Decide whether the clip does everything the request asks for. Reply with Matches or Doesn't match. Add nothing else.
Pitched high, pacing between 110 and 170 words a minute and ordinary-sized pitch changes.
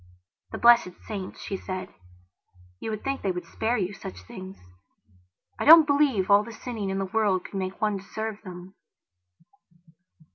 Matches